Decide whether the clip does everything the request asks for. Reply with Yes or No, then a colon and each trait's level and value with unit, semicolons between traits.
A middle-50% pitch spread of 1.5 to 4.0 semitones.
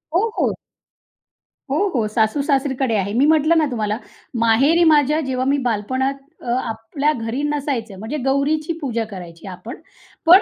No: average, 4.9 semitones